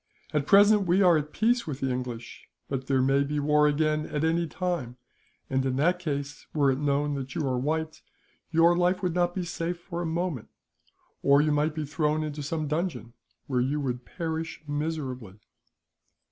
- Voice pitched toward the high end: No, medium, 150 Hz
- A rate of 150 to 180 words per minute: No, average, 190 wpm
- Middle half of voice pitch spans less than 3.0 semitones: No, average, 3.4 semitones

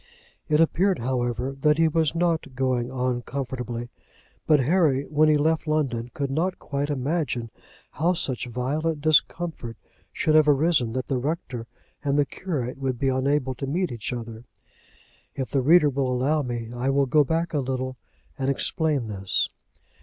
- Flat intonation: No, average, 3.7 semitones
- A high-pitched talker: No, low, 135 Hz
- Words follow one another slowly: No, average, 165 wpm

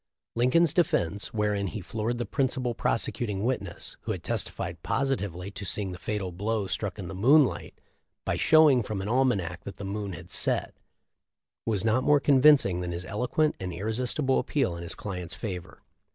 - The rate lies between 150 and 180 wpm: Yes, average, 170 wpm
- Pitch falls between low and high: No, low, 105 Hz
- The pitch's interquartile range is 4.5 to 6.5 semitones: Yes, average, 5.1 semitones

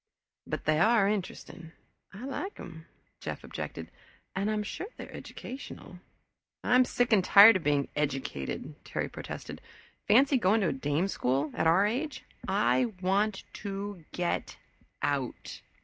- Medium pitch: No, high, 195 Hz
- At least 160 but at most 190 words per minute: No, average, 145 wpm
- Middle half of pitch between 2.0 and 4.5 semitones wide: No, wide, 5.4 semitones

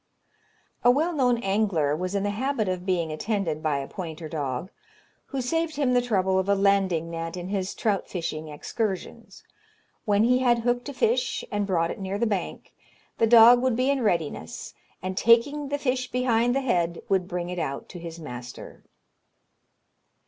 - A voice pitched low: No, high, 200 Hz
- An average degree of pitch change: No, wide, 6.2 semitones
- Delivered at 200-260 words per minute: No, average, 180 wpm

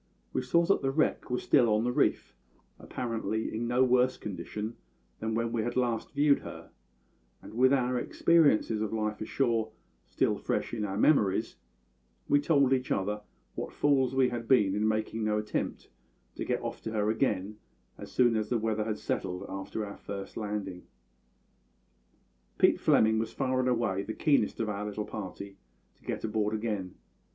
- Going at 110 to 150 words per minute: No, average, 175 wpm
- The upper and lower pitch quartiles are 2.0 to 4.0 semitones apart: Yes, average, 3.1 semitones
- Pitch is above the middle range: No, low, 110 Hz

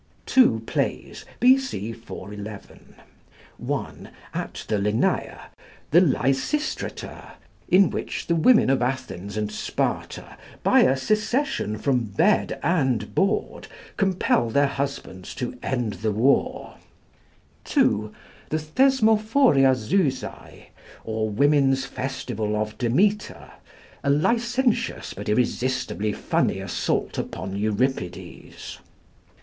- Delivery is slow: Yes, slow, 100 wpm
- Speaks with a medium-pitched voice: No, low, 130 Hz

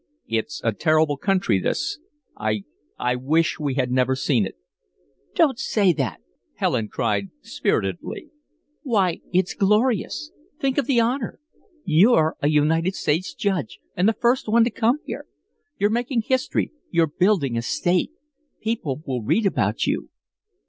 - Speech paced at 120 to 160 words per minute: Yes, average, 145 wpm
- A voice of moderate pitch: Yes, medium, 165 Hz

